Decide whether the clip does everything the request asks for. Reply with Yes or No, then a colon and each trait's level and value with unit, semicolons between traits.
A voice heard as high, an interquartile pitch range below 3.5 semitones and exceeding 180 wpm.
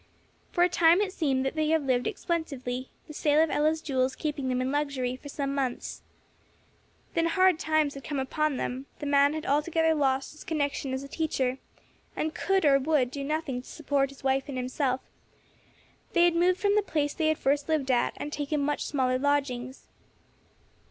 Yes: very high, 285 Hz; average, 2.9 semitones; average, 190 wpm